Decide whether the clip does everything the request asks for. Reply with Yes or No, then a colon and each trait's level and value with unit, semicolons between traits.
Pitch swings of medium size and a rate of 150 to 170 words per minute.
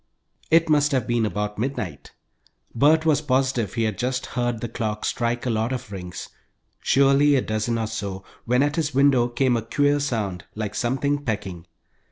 No: average, 4.3 semitones; average, 180 wpm